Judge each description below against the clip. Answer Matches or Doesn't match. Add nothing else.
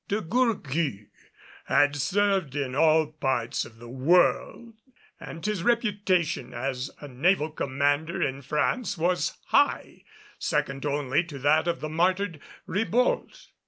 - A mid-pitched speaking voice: Matches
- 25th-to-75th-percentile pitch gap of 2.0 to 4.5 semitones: Doesn't match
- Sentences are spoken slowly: Matches